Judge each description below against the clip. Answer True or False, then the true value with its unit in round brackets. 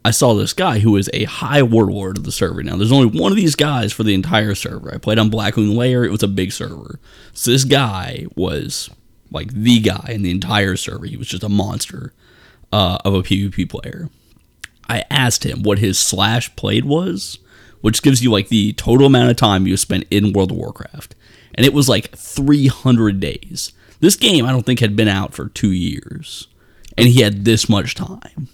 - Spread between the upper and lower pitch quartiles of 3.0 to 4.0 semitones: True (3.7 semitones)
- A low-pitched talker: True (110 Hz)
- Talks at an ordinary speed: False (210 wpm)